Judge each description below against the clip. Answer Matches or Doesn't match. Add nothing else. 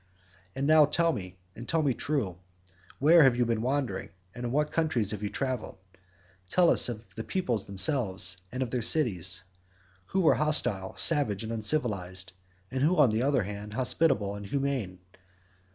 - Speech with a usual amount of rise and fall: Doesn't match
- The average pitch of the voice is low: Matches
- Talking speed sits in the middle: Matches